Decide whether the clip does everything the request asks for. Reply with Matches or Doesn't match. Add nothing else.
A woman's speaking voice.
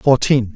Doesn't match